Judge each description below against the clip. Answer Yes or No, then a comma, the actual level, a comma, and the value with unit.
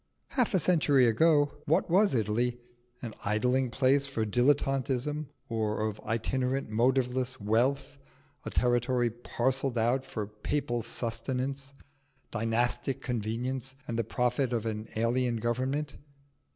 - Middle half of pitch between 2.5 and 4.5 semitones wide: Yes, average, 2.9 semitones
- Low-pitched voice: Yes, low, 125 Hz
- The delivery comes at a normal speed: No, slow, 120 wpm